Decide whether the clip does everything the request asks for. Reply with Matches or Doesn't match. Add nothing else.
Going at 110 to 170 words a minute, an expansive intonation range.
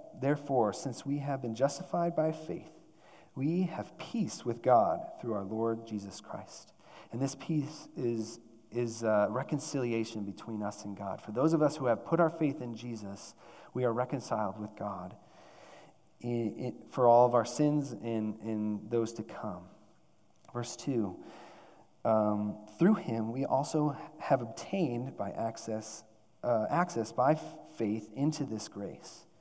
Doesn't match